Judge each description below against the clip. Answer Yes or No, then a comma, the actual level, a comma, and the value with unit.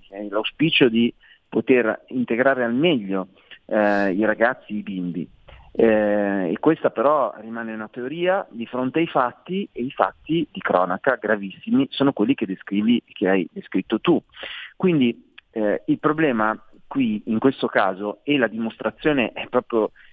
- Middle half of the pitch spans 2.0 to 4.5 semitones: No, average, 5.0 semitones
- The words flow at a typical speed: Yes, average, 150 wpm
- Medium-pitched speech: No, low, 115 Hz